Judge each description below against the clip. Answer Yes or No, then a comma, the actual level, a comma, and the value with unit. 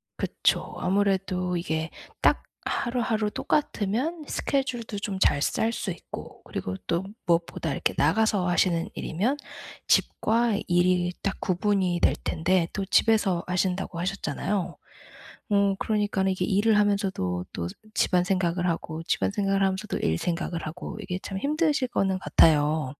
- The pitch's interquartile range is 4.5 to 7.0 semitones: No, average, 3.2 semitones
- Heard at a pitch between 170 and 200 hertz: Yes, high, 190 Hz